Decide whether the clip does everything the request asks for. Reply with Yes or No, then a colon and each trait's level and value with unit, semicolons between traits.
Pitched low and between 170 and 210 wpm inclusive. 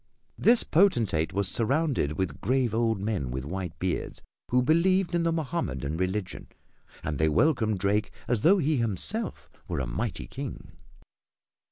No: low, 110 Hz; average, 150 wpm